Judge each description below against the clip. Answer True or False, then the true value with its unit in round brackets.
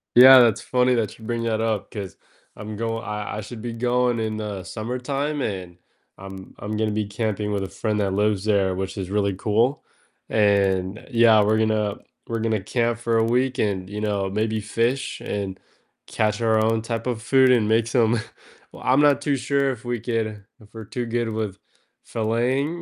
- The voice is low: True (110 Hz)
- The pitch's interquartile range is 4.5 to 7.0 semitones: False (2.4 semitones)